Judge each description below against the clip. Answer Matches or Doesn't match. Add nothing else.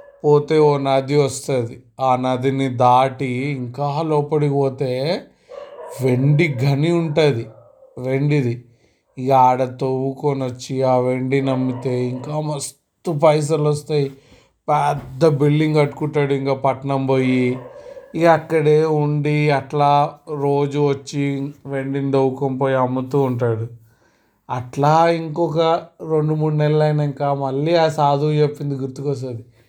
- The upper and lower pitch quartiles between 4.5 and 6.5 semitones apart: Doesn't match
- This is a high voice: Doesn't match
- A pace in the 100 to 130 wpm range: Matches